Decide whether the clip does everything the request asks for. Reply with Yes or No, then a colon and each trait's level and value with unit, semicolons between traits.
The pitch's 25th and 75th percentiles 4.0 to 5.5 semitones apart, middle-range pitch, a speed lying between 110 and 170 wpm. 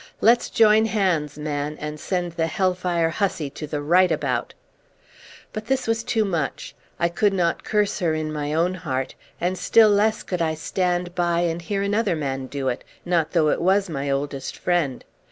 No: average, 4.5 semitones; medium, 175 Hz; average, 185 wpm